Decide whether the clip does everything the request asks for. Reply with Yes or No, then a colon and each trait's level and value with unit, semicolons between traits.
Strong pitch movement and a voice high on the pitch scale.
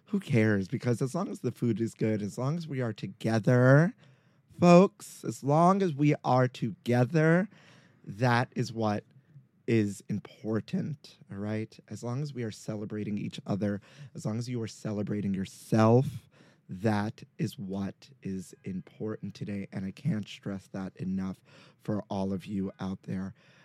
No: wide, 5.9 semitones; low, 120 Hz